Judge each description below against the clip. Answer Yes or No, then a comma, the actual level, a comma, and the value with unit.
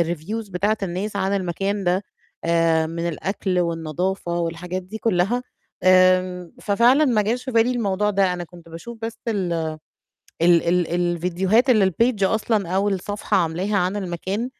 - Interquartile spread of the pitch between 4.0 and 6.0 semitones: No, average, 3.3 semitones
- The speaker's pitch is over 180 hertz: Yes, high, 190 Hz